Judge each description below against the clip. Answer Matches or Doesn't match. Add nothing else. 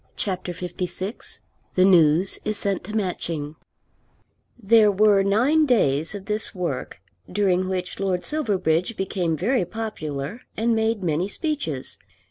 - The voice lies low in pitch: Doesn't match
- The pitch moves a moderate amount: Matches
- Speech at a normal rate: Doesn't match